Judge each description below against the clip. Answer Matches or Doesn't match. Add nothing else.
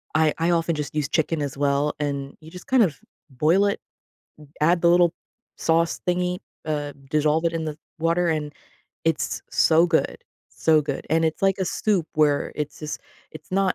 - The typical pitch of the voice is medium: Matches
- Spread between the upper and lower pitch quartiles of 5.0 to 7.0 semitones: Doesn't match